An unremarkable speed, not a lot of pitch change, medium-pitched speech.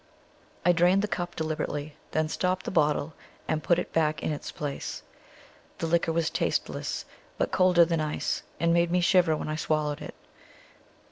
Yes: average, 175 wpm; narrow, 2.3 semitones; medium, 165 Hz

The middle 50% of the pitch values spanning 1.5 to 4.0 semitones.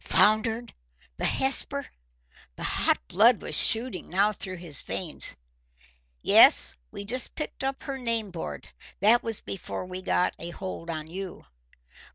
No: average, 4.6 semitones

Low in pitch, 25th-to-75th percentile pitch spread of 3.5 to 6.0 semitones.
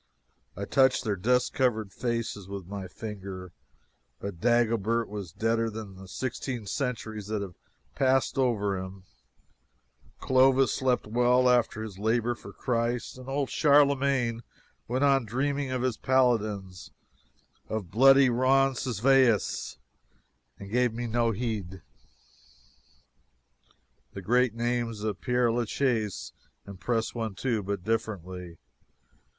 Yes: low, 115 Hz; average, 3.8 semitones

